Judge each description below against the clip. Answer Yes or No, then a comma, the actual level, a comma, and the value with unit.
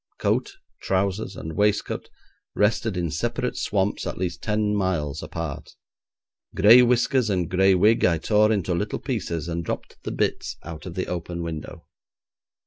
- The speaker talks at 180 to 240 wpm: No, average, 150 wpm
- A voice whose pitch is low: Yes, very low, 95 Hz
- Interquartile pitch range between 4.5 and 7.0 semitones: No, average, 3.9 semitones